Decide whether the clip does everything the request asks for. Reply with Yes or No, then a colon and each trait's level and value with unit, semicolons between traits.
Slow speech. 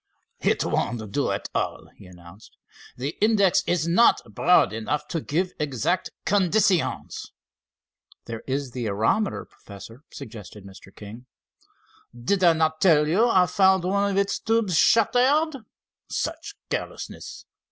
Yes: slow, 130 wpm